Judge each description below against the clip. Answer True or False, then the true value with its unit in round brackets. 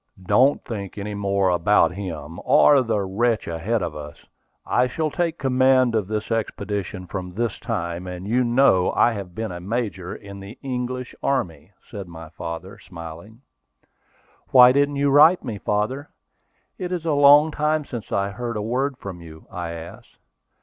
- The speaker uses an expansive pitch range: True (5.8 semitones)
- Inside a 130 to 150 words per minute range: False (170 wpm)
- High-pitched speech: False (105 Hz)